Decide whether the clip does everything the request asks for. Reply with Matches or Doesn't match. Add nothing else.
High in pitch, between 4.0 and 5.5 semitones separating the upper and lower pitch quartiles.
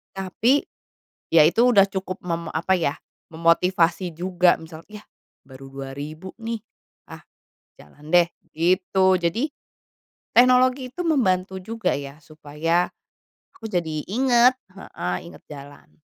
Doesn't match